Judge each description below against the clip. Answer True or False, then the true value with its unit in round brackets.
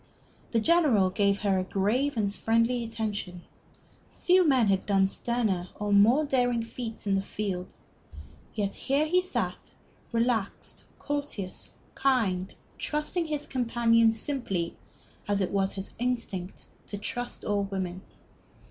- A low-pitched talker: False (225 Hz)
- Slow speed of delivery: True (130 wpm)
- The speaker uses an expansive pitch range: False (4.2 semitones)